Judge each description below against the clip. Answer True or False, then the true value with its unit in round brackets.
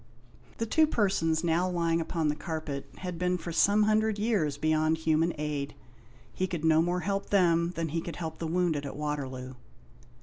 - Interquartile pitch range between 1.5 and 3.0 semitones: True (2.6 semitones)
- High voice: False (165 Hz)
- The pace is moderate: True (180 wpm)